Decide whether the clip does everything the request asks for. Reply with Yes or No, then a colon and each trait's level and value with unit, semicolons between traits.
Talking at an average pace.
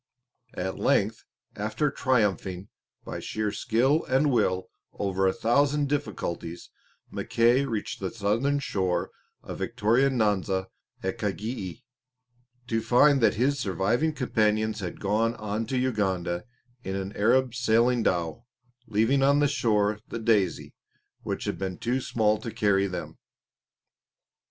No: slow, 130 wpm